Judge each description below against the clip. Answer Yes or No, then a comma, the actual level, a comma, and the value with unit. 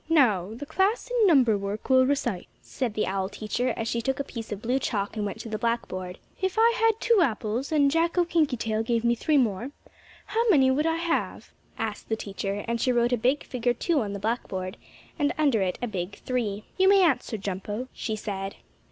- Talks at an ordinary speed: No, fast, 215 wpm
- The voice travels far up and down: Yes, wide, 5.7 semitones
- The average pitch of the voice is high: Yes, high, 240 Hz